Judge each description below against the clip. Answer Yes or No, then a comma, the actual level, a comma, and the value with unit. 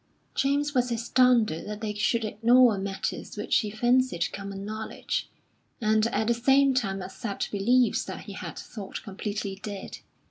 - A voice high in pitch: Yes, high, 220 Hz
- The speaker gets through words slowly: No, average, 150 wpm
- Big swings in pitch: No, average, 3.6 semitones